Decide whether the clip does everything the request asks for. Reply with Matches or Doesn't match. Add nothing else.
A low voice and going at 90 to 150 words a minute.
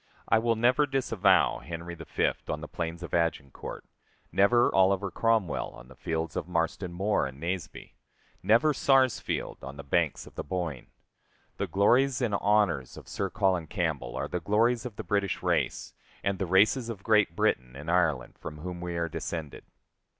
Doesn't match